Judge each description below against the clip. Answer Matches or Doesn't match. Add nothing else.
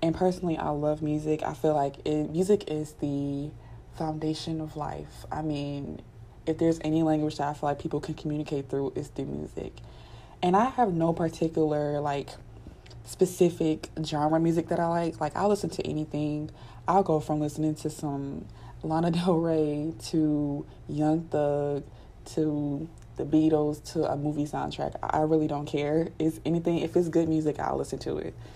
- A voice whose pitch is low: Doesn't match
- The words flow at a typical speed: Matches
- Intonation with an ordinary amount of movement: Doesn't match